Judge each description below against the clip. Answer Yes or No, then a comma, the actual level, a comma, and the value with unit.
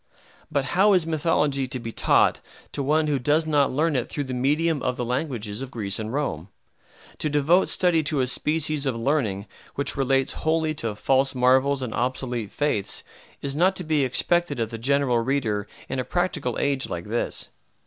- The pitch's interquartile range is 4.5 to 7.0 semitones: No, average, 3.7 semitones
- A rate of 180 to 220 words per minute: Yes, average, 190 wpm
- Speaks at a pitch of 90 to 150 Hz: Yes, low, 135 Hz